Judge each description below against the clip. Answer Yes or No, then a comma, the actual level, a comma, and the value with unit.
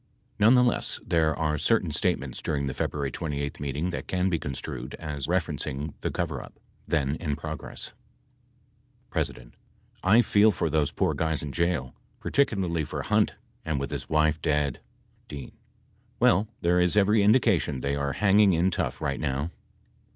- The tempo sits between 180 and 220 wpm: No, average, 155 wpm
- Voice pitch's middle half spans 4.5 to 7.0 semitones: No, average, 4.1 semitones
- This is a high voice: No, very low, 80 Hz